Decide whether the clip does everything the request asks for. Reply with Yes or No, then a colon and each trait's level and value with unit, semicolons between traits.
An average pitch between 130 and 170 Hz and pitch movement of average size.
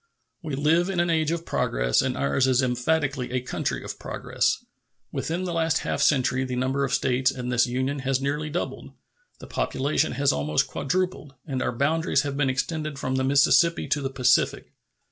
Yes: medium, 140 Hz; average, 3.5 semitones